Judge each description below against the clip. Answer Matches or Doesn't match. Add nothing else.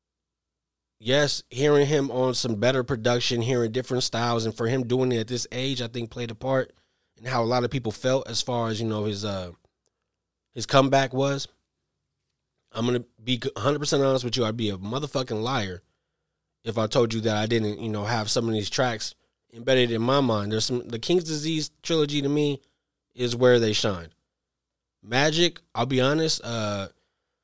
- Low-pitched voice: Matches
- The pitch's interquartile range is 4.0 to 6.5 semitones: Doesn't match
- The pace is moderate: Matches